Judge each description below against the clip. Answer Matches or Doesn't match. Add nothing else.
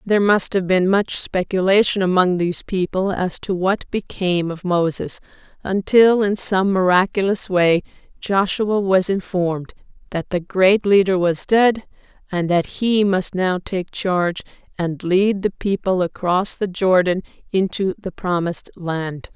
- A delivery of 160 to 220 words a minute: Doesn't match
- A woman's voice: Matches